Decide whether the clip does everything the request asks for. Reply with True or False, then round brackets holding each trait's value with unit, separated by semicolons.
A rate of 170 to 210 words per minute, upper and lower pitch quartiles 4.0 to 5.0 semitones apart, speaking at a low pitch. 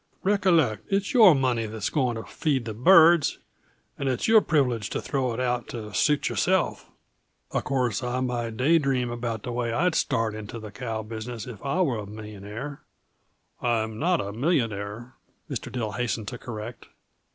True (175 wpm; 4.3 semitones; 120 Hz)